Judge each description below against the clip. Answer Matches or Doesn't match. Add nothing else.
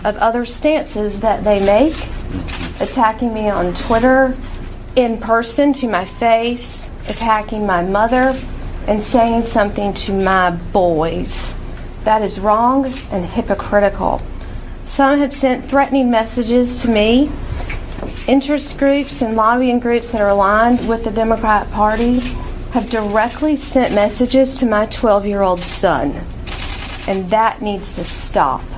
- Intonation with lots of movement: Doesn't match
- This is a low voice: Doesn't match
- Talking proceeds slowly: Matches